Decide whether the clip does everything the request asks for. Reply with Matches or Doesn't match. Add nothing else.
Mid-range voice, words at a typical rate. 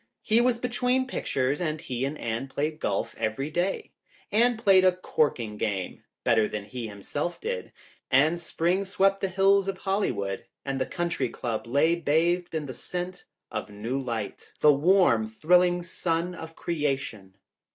Matches